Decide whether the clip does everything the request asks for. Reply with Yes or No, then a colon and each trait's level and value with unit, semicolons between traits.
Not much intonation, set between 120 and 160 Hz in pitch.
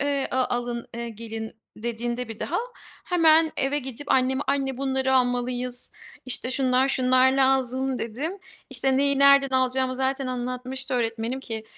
No: narrow, 1.7 semitones; very high, 260 Hz